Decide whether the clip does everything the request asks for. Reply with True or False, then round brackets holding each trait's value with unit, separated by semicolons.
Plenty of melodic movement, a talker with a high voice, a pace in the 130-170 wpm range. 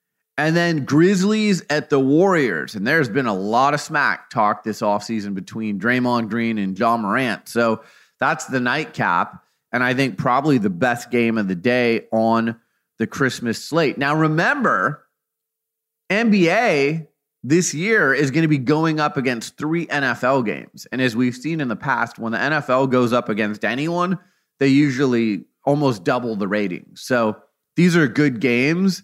False (5.7 semitones; 135 Hz; 165 wpm)